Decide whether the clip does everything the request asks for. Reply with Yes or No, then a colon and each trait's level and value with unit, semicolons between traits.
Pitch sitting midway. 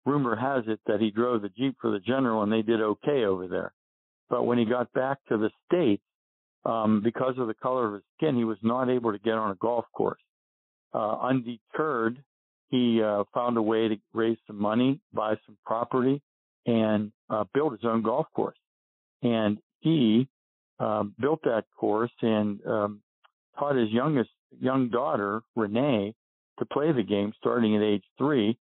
No: low, 110 Hz